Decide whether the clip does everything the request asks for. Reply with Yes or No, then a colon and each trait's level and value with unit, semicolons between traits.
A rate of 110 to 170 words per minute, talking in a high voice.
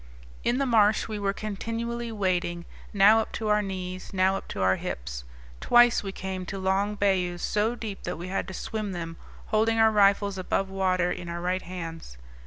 No: average, 195 wpm; high, 195 Hz